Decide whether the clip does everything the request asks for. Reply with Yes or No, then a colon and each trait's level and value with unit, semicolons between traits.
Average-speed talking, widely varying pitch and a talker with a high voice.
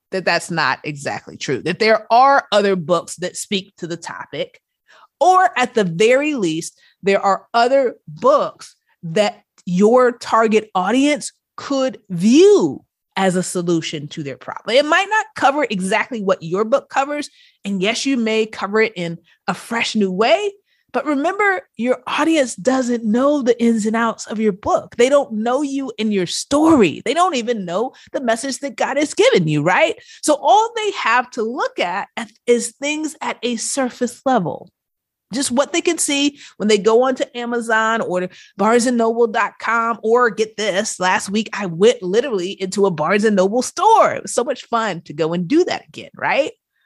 Yes: average, 180 wpm; wide, 5.9 semitones; high, 230 Hz